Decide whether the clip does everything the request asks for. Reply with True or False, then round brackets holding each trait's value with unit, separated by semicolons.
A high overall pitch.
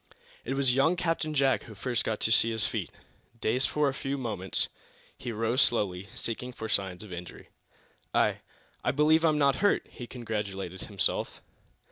False (120 Hz)